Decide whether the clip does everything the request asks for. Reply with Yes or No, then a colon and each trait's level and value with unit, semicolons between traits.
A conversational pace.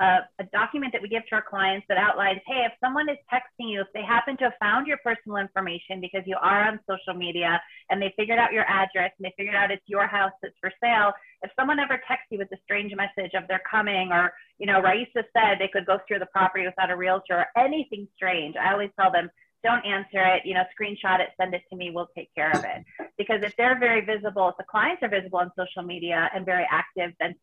No: fast, 250 wpm